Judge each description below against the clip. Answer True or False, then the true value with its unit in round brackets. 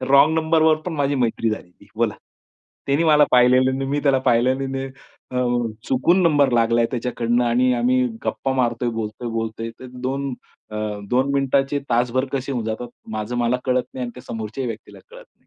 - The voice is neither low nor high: False (125 Hz)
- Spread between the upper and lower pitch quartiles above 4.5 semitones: False (2.6 semitones)